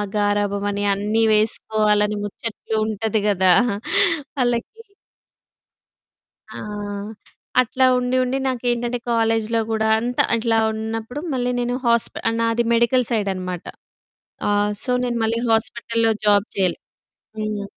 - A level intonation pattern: Yes, narrow, 2.3 semitones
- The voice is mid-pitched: No, high, 225 Hz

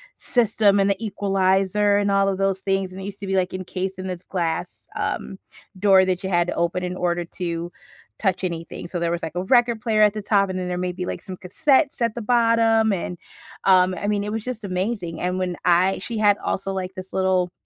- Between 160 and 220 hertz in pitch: Yes, high, 190 Hz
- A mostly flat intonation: Yes, narrow, 2.2 semitones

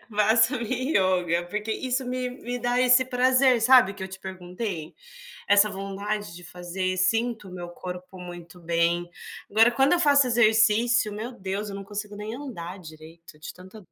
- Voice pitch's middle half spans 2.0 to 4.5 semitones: No, average, 5.1 semitones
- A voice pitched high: Yes, high, 210 Hz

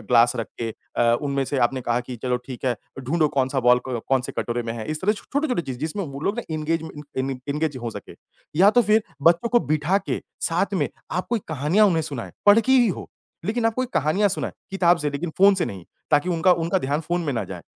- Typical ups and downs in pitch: No, wide, 7.0 semitones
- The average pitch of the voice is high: No, medium, 155 Hz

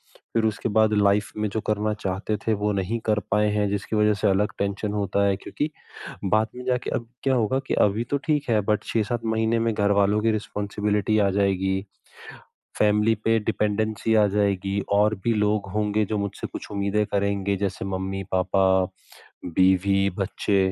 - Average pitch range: No, narrow, 1.6 semitones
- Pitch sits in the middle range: No, low, 105 Hz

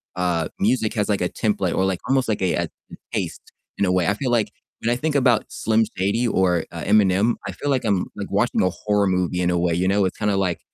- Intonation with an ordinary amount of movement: Yes, average, 3.5 semitones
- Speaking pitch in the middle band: No, low, 100 Hz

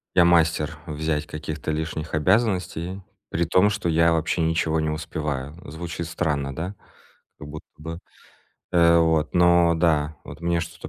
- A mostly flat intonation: Yes, narrow, 1.8 semitones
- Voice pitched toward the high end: No, very low, 80 Hz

